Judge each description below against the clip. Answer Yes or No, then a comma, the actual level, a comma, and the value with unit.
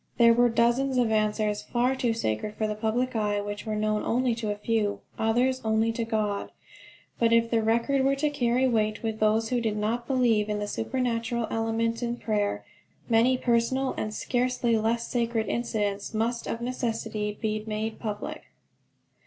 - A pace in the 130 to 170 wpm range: No, average, 180 wpm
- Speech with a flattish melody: Yes, narrow, 2.0 semitones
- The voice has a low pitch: No, high, 225 Hz